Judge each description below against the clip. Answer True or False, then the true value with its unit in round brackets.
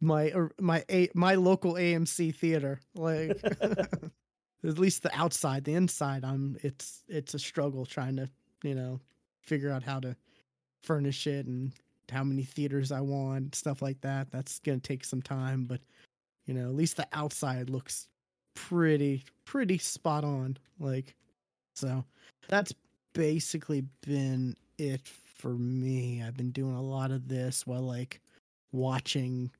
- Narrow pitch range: False (3.4 semitones)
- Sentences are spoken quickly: False (150 wpm)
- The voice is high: False (140 Hz)